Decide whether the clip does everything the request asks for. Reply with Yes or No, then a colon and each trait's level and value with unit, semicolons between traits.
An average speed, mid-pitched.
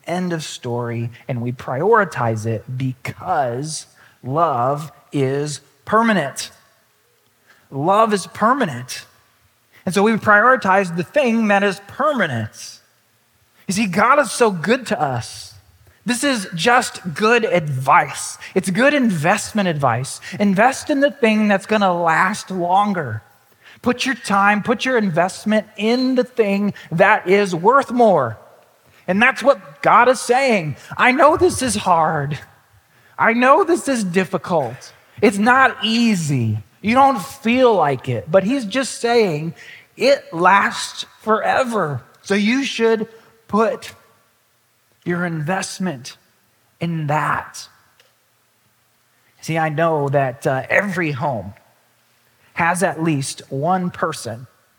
No: slow, 125 wpm; medium, 180 Hz